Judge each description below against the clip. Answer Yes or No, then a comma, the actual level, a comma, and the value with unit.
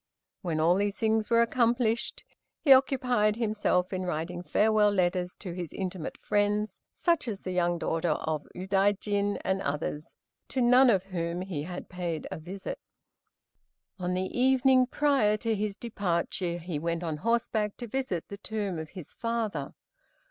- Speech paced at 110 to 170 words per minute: Yes, average, 155 wpm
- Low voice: No, high, 195 Hz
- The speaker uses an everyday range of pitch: Yes, average, 4.3 semitones